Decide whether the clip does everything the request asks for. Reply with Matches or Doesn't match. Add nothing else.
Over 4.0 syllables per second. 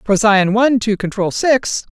Matches